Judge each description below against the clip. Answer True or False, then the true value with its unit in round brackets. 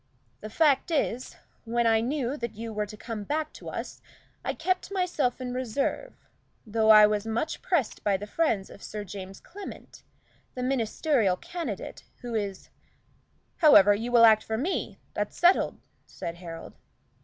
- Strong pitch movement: True (5.7 semitones)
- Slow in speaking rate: False (165 wpm)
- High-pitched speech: True (230 Hz)